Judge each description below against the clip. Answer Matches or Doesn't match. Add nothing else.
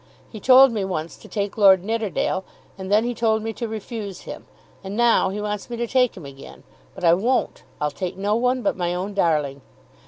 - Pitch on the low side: Doesn't match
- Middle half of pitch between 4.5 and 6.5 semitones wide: Doesn't match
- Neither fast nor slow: Doesn't match